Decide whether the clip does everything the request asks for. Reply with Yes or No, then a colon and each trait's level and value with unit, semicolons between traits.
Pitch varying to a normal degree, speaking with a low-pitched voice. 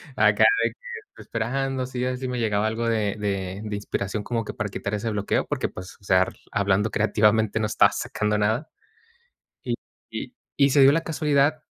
Yes: average, 3.8 semitones; low, 110 Hz